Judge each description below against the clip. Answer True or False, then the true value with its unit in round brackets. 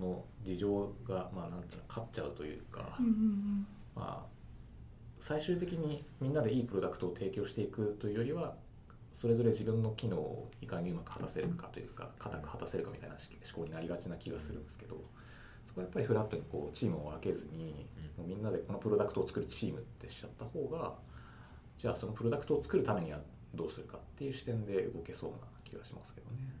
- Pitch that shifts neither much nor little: False (6.6 semitones)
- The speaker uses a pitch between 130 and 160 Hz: False (115 Hz)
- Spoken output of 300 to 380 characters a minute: False (415 characters per minute)